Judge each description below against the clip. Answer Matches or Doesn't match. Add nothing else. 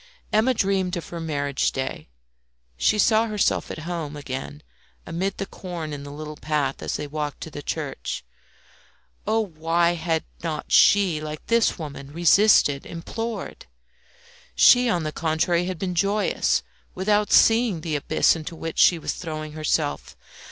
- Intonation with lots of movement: Doesn't match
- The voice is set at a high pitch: Doesn't match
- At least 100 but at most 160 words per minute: Matches